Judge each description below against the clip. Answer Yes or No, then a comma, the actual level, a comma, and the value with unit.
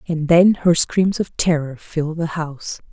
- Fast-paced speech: No, average, 185 wpm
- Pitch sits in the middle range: Yes, medium, 165 Hz